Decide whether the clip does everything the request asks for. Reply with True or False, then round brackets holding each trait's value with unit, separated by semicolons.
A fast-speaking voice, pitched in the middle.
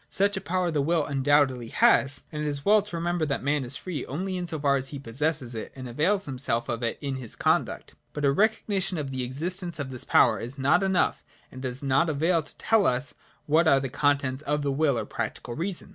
True (235 wpm; 145 Hz)